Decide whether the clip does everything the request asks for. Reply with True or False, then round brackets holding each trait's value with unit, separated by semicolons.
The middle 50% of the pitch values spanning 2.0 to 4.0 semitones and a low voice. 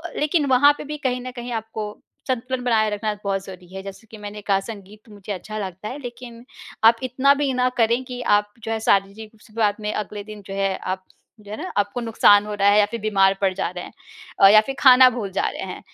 False (3.5 semitones; 215 Hz)